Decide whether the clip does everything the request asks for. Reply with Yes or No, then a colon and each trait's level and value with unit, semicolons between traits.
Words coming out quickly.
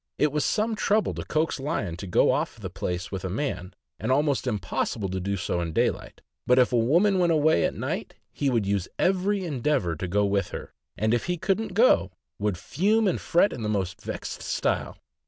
Yes: fast, 210 wpm